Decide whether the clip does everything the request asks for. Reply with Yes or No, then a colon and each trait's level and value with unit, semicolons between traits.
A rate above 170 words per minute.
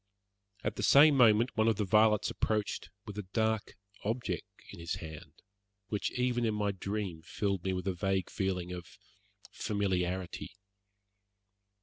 No: average, 145 wpm